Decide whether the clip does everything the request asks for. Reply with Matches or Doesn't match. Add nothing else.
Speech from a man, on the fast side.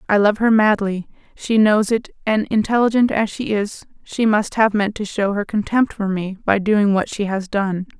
Doesn't match